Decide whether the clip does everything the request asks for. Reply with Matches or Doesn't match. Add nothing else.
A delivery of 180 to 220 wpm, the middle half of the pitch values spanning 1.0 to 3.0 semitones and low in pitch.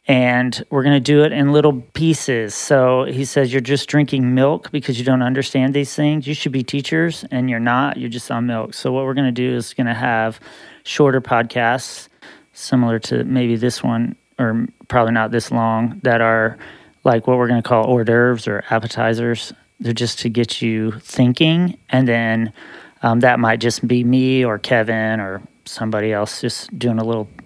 Matches